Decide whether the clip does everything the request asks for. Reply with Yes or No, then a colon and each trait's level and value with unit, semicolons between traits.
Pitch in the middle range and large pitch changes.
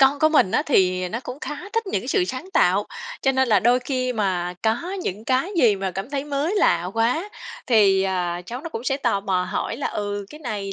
No: high, 235 Hz; wide, 6.1 semitones